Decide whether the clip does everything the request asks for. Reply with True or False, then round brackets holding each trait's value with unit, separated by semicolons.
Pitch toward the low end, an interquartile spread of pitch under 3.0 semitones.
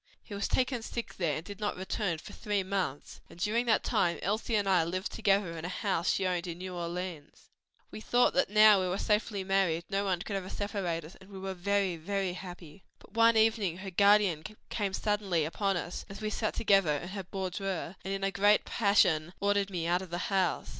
False (195 Hz; 2.6 semitones)